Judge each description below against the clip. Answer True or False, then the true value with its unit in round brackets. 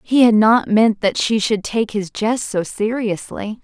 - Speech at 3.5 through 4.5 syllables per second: True (4.0 syllables/s)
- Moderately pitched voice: False (215 Hz)